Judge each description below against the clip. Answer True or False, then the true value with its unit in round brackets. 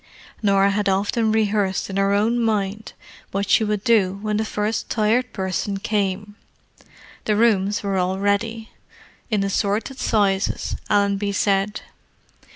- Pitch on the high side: True (205 Hz)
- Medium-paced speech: False (130 wpm)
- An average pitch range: False (1.6 semitones)